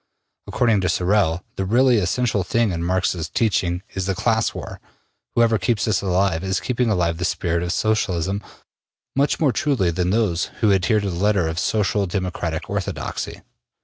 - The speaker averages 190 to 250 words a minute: No, average, 170 wpm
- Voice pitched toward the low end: Yes, very low, 95 Hz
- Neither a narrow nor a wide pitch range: Yes, average, 3.8 semitones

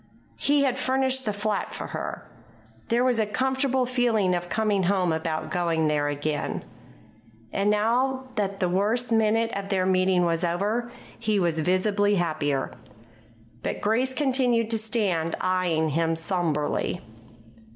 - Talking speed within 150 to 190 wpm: No, average, 140 wpm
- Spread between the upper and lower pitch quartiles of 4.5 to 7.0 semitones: Yes, average, 5.2 semitones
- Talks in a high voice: Yes, high, 200 Hz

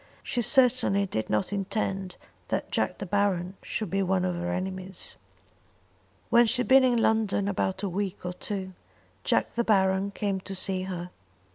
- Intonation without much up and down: Yes, narrow, 1.9 semitones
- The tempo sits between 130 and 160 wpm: No, average, 170 wpm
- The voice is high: Yes, high, 195 Hz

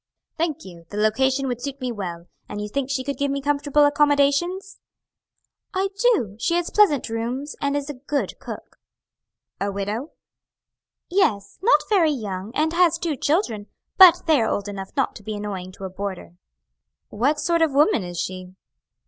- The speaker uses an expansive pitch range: Yes, wide, 6.7 semitones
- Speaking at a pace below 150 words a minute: No, average, 175 wpm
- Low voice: No, very high, 270 Hz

